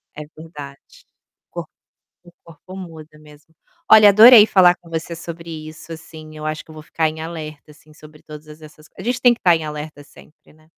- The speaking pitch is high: No, medium, 155 Hz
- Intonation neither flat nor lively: No, narrow, 1.8 semitones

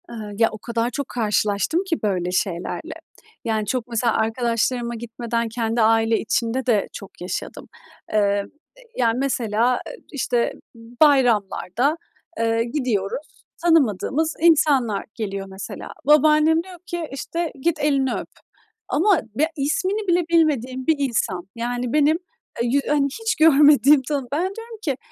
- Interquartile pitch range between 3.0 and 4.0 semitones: No, average, 5.1 semitones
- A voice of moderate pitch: No, very high, 250 Hz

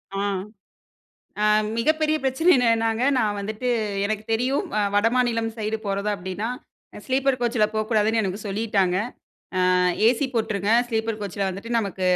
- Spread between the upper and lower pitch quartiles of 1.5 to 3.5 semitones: Yes, average, 2.8 semitones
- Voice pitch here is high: Yes, high, 220 Hz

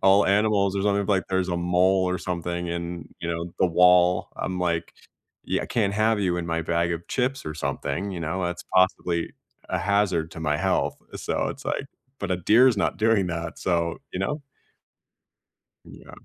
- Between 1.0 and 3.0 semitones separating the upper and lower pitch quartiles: Yes, narrow, 2.6 semitones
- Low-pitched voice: Yes, very low, 90 Hz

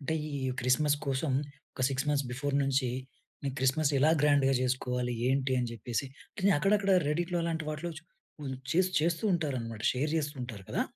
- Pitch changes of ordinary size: Yes, average, 3.1 semitones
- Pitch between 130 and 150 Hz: Yes, medium, 140 Hz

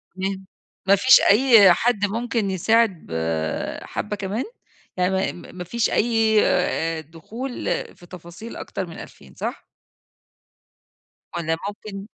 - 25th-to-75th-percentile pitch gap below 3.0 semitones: No, average, 4.4 semitones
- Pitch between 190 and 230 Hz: Yes, high, 195 Hz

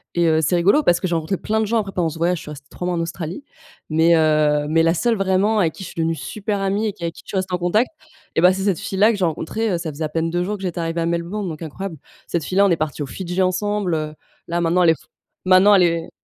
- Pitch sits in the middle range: Yes, medium, 175 Hz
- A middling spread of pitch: Yes, average, 3.0 semitones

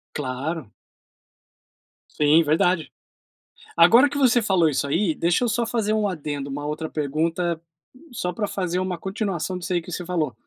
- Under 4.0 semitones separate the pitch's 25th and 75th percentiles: No, average, 4.3 semitones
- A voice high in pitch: No, medium, 175 Hz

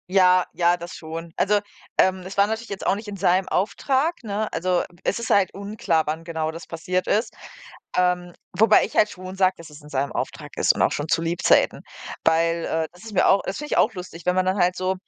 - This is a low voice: No, medium, 185 Hz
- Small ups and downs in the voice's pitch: No, average, 3.1 semitones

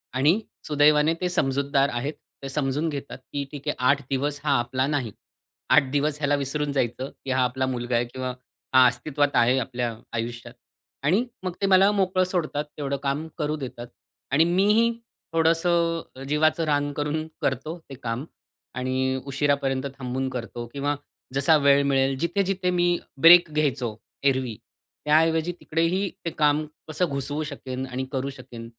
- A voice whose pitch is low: No, medium, 145 Hz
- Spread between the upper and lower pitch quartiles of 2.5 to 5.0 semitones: Yes, average, 3.2 semitones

